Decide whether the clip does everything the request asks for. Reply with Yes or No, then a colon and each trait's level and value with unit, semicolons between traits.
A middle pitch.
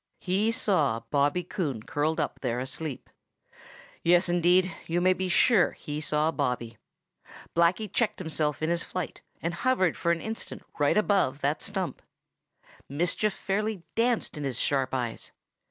Yes: medium, 170 Hz